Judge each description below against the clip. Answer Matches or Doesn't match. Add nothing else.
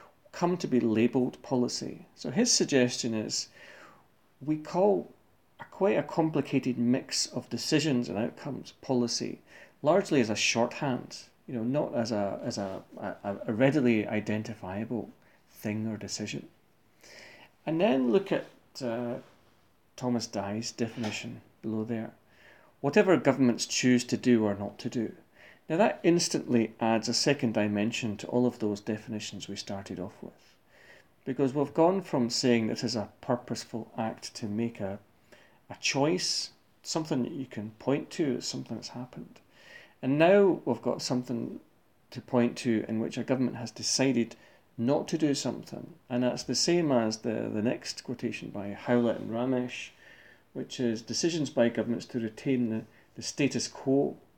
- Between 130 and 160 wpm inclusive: Matches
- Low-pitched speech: Matches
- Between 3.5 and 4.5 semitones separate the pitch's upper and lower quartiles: Doesn't match